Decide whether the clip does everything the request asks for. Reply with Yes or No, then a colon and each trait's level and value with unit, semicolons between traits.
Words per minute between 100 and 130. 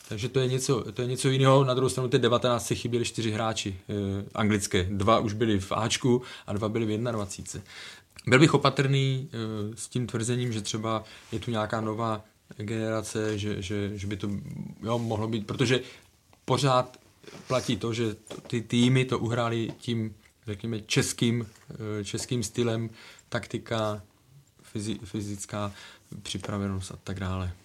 No: average, 160 wpm